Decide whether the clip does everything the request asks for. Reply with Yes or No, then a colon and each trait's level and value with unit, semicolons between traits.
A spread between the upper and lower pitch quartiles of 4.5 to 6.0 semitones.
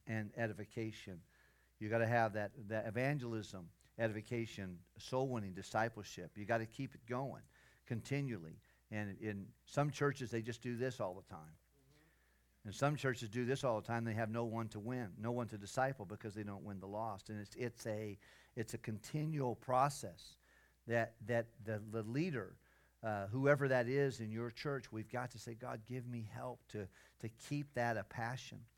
No: average, 2.9 semitones